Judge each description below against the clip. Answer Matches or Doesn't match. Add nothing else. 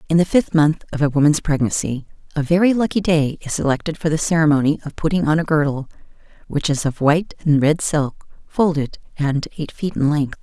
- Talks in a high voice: Doesn't match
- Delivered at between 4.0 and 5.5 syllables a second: Doesn't match